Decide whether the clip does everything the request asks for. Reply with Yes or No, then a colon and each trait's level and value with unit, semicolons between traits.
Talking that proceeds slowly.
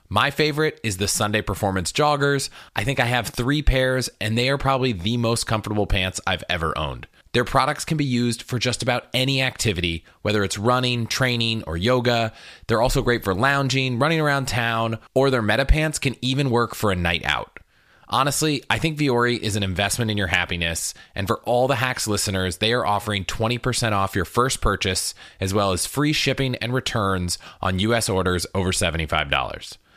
No: average, 190 wpm